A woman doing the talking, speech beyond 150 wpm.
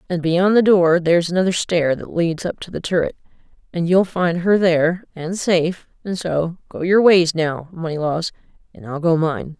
Yes: female; average, 175 wpm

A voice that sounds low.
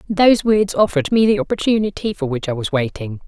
No: medium, 185 Hz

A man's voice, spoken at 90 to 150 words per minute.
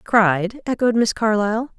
No: female; slow, 135 wpm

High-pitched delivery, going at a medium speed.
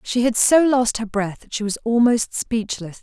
No: high, 230 Hz; fast, 220 wpm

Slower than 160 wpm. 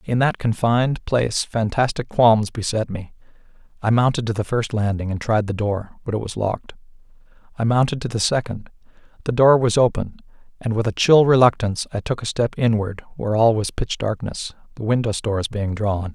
No: average, 190 wpm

